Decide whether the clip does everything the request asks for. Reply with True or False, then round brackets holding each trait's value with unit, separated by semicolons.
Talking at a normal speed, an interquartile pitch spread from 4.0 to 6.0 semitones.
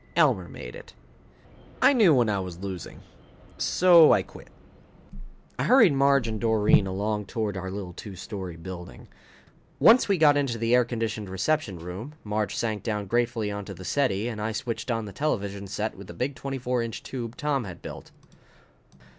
True (175 wpm; 4.7 semitones)